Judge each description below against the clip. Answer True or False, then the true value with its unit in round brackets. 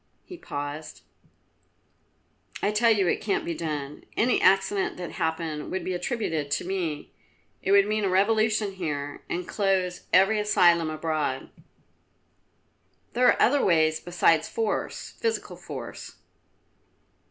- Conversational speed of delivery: False (130 wpm)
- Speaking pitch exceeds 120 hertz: True (185 Hz)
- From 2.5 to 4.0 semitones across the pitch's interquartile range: False (4.8 semitones)